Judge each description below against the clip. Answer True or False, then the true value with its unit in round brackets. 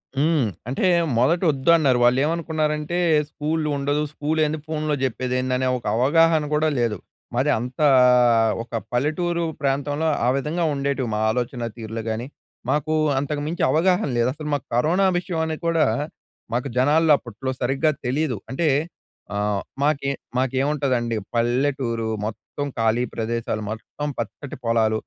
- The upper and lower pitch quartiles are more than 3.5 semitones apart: True (4.1 semitones)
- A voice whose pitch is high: False (140 Hz)